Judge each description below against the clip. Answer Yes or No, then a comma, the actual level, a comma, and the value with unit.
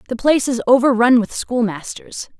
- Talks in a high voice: Yes, high, 240 Hz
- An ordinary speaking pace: Yes, average, 150 wpm